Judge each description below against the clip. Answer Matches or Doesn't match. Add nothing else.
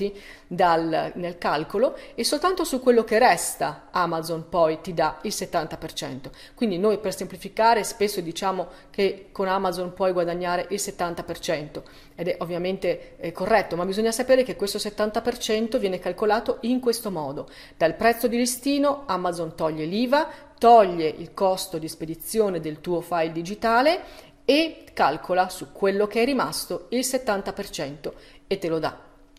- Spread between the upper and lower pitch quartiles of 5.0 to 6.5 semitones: Matches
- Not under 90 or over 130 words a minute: Doesn't match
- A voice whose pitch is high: Matches